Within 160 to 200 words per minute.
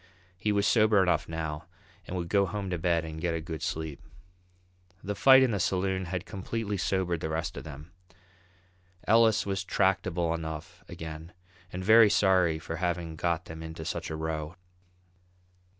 Yes: average, 165 wpm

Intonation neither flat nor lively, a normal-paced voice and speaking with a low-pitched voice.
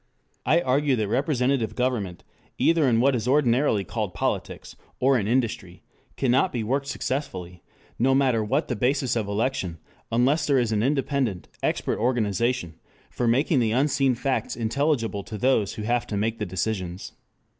Yes: average, 4.0 semitones; average, 160 wpm; low, 120 Hz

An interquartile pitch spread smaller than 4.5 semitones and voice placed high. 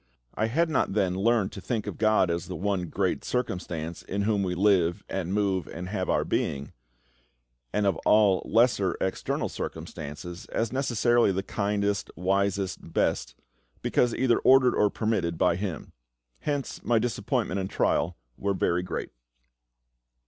No: average, 3.5 semitones; low, 100 Hz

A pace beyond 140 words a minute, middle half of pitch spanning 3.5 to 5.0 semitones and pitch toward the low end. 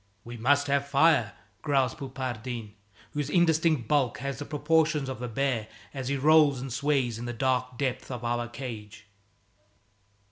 No: average, 155 wpm; average, 3.1 semitones; low, 130 Hz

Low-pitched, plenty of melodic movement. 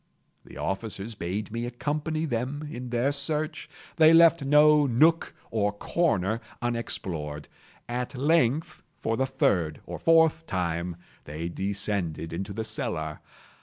Yes: low, 120 Hz; wide, 7.4 semitones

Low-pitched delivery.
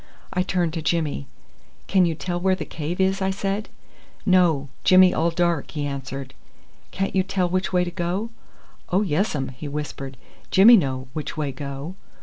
No: medium, 175 Hz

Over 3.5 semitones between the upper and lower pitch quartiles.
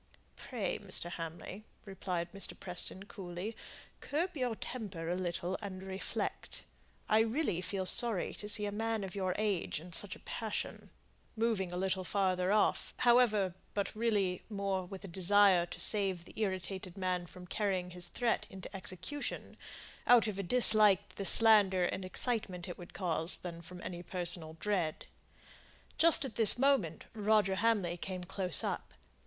No: average, 3.0 semitones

